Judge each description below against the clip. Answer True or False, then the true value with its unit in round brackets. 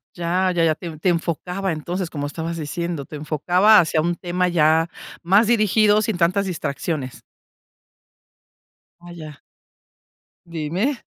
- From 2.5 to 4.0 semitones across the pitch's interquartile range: True (2.8 semitones)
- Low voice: False (170 Hz)